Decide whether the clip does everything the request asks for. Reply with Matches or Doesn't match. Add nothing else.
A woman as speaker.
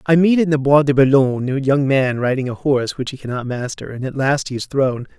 Doesn't match